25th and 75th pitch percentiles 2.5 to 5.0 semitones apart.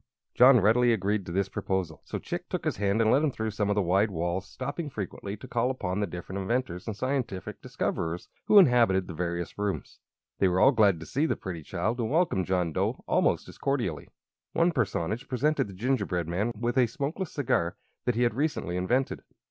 No: wide, 5.6 semitones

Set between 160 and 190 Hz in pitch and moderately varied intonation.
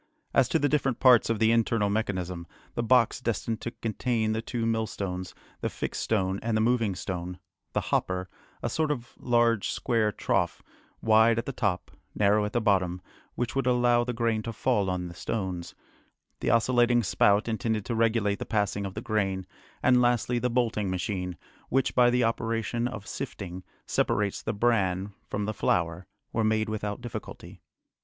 No: low, 110 Hz; average, 3.1 semitones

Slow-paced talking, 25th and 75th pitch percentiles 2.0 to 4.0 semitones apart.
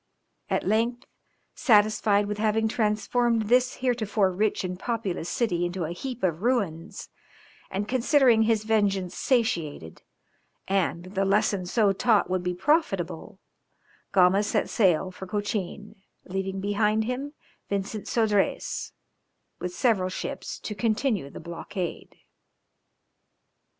Yes: slow, 120 wpm; average, 3.4 semitones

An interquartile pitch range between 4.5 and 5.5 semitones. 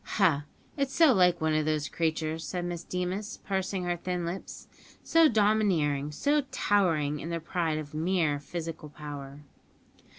No: average, 3.8 semitones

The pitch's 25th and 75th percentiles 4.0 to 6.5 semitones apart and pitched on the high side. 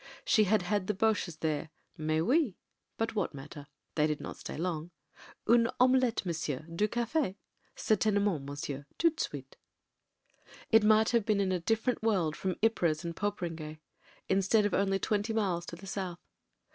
Yes: average, 5.0 semitones; high, 195 Hz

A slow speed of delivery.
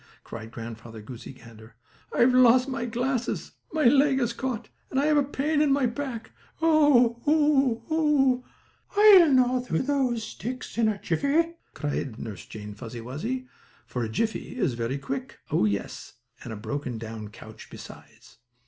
No: average, 165 wpm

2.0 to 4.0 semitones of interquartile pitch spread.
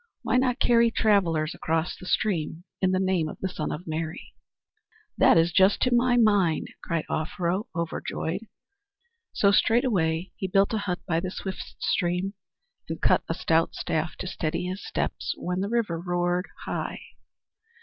Yes: average, 3.5 semitones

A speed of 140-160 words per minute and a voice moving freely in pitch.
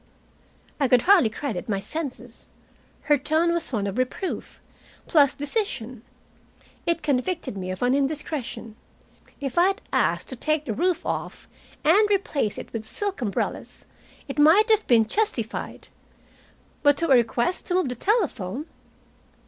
Yes: average, 150 wpm; wide, 6.3 semitones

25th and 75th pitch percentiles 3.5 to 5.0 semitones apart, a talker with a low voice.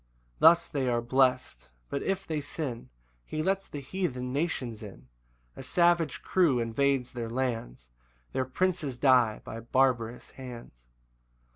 Yes: average, 4.7 semitones; low, 130 Hz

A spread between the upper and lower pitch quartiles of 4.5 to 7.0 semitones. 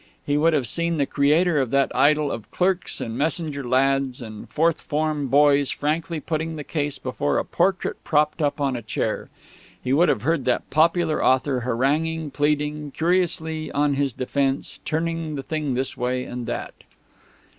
No: average, 3.0 semitones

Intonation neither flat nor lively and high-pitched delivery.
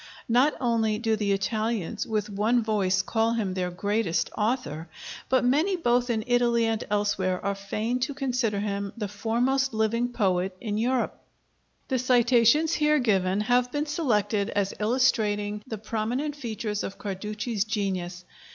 Yes: average, 3.3 semitones; high, 220 Hz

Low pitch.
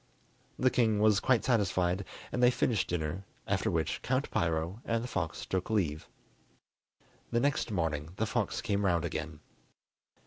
Yes: low, 100 Hz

